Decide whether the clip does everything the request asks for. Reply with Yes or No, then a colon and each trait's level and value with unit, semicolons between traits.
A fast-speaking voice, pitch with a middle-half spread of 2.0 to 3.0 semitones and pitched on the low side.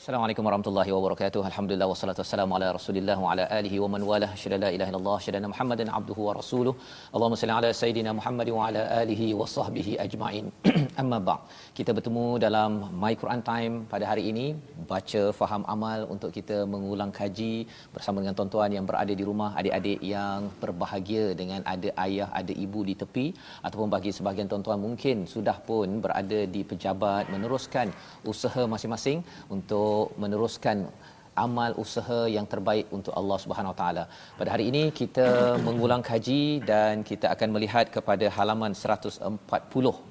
Yes: fast, 160 wpm; narrow, 2.5 semitones; low, 105 Hz